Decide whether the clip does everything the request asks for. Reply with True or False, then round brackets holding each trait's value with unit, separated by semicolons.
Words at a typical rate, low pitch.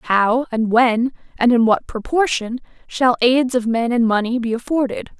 False (175 wpm; 240 Hz)